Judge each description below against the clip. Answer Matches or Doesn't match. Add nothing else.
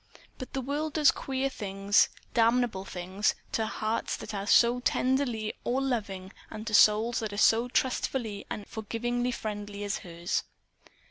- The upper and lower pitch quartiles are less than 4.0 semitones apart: Matches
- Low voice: Doesn't match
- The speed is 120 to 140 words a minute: Doesn't match